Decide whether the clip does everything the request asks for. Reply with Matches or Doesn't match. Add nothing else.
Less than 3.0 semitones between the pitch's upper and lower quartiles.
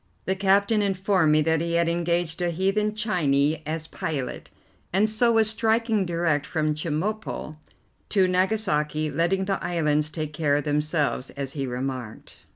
Doesn't match